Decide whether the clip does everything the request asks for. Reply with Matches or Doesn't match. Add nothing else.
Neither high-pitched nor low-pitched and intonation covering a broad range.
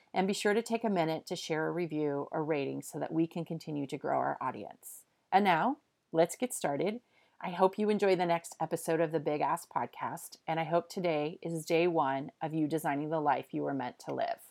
Doesn't match